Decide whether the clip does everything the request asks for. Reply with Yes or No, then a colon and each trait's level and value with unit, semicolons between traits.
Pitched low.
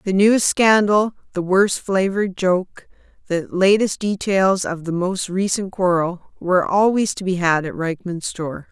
No: high, 190 Hz